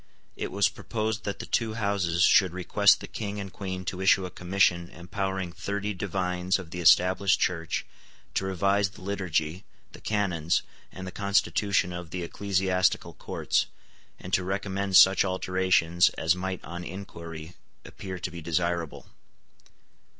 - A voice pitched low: Yes, very low, 95 Hz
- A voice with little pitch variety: Yes, narrow, 2.2 semitones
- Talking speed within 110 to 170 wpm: Yes, average, 150 wpm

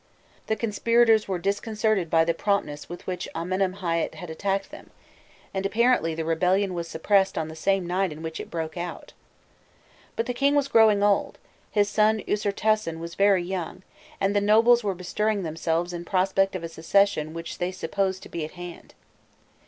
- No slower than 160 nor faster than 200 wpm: Yes, average, 175 wpm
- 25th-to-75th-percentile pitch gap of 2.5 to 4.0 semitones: Yes, average, 3.6 semitones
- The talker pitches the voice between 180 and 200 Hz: Yes, high, 190 Hz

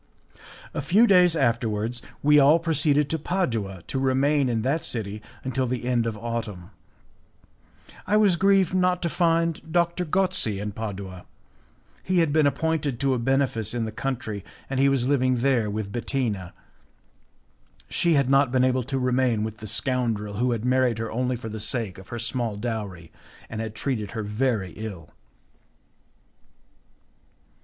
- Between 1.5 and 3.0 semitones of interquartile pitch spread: No, average, 4.6 semitones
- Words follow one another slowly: No, average, 160 wpm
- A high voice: No, low, 125 Hz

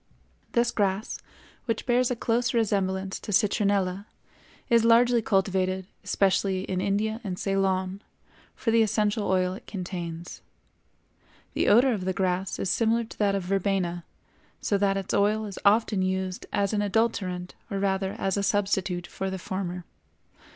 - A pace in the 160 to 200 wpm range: No, average, 150 wpm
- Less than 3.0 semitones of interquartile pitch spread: Yes, narrow, 2.4 semitones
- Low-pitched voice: No, high, 195 Hz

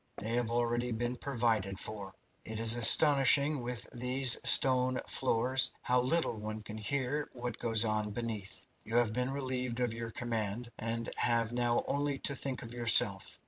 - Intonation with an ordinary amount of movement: No, narrow, 2.1 semitones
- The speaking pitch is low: Yes, low, 120 Hz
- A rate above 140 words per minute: Yes, average, 165 wpm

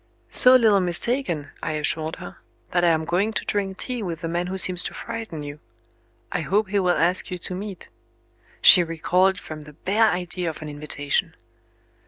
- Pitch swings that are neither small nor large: Yes, average, 3.7 semitones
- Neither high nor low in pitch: Yes, medium, 180 Hz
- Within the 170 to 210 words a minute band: Yes, average, 195 wpm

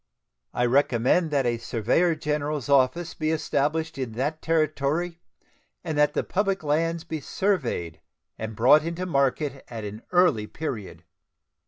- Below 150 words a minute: Yes, average, 140 wpm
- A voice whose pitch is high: No, medium, 150 Hz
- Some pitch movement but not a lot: Yes, average, 4.6 semitones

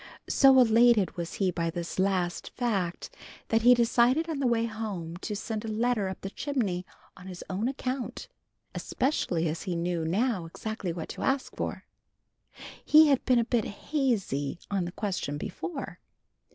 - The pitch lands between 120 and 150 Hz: No, high, 215 Hz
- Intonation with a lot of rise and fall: Yes, wide, 5.7 semitones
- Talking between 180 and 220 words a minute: No, average, 165 wpm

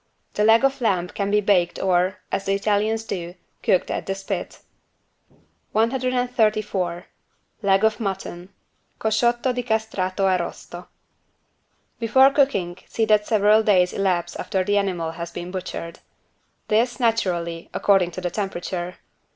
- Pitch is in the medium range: No, high, 200 Hz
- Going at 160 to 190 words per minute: No, slow, 135 wpm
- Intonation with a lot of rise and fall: No, average, 3.6 semitones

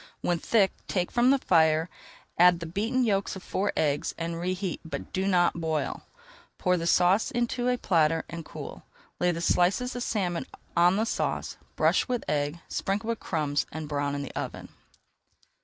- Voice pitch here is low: No, medium, 175 Hz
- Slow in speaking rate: No, average, 175 wpm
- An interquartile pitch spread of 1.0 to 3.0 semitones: No, average, 3.9 semitones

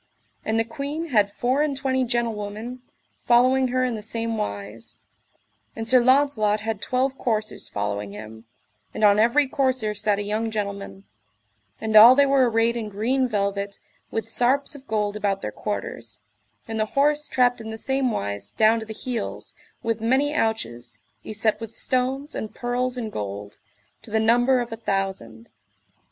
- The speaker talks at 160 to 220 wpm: Yes, average, 170 wpm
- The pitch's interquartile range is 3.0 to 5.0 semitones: Yes, average, 3.7 semitones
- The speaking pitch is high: Yes, high, 225 Hz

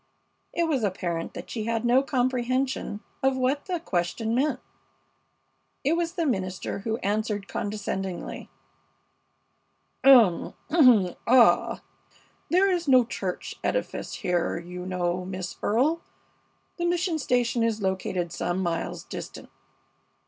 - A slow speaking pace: Yes, slow, 120 wpm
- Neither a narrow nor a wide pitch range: No, wide, 6.3 semitones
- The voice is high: Yes, high, 230 Hz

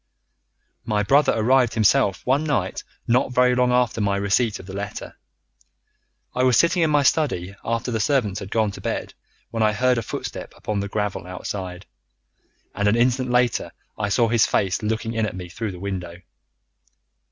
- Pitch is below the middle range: Yes, low, 110 Hz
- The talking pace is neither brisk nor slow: Yes, average, 180 wpm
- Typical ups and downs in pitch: Yes, average, 4.0 semitones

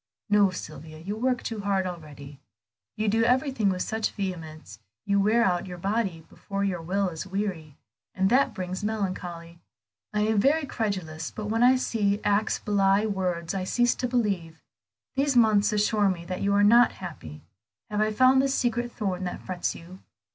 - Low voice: No, high, 200 Hz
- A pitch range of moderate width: Yes, average, 3.6 semitones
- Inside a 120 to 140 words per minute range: No, average, 180 wpm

